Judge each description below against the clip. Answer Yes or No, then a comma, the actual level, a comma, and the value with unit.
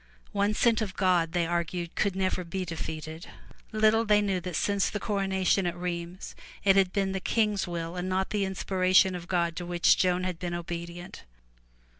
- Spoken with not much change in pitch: Yes, narrow, 2.1 semitones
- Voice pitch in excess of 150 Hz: Yes, medium, 185 Hz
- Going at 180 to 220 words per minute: Yes, average, 190 wpm